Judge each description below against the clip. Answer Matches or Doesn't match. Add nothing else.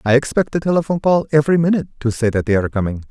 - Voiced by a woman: Doesn't match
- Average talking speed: Doesn't match